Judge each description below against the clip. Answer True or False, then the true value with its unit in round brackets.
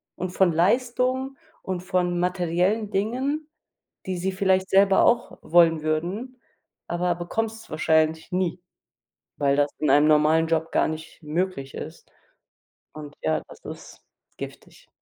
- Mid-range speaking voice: True (180 Hz)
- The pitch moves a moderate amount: True (3.9 semitones)